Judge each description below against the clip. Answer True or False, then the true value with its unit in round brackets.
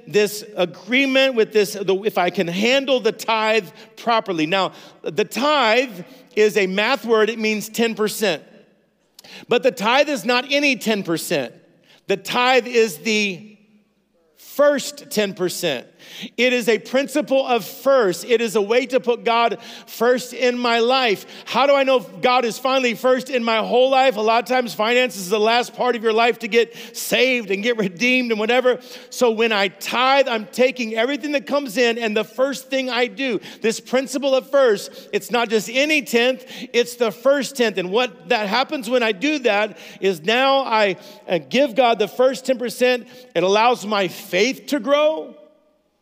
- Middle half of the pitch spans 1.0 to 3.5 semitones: True (3.2 semitones)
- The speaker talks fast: False (175 wpm)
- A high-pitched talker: True (235 Hz)